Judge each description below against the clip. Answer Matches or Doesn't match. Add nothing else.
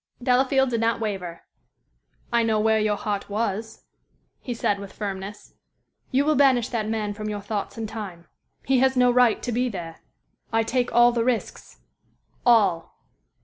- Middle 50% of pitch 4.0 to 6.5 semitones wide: Doesn't match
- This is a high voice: Matches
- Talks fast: Doesn't match